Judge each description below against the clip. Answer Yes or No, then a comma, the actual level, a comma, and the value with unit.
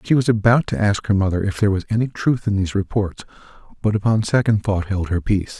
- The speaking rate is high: Yes, fast, 235 wpm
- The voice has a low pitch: Yes, low, 105 Hz